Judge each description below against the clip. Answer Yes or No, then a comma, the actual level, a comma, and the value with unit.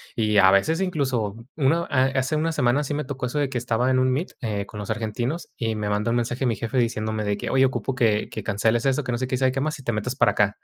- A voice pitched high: No, low, 125 Hz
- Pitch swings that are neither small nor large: Yes, average, 3.7 semitones